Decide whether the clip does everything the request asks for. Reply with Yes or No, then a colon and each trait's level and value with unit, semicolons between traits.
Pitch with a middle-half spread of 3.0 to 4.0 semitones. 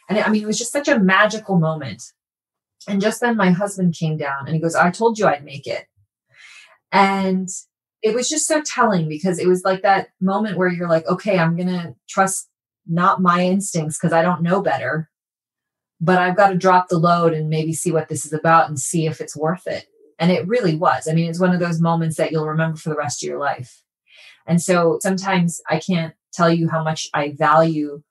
Yes: average, 3.3 semitones